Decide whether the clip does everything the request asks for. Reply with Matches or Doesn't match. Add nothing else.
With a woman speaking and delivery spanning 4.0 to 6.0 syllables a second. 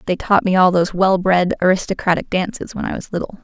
Doesn't match